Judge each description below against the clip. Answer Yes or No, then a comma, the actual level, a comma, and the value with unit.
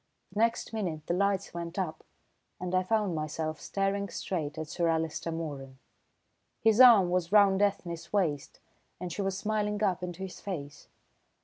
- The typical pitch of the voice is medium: Yes, medium, 180 Hz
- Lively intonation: No, average, 3.7 semitones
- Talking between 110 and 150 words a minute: No, average, 165 wpm